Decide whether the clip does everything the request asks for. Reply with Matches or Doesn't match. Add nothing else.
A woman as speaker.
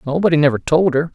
Doesn't match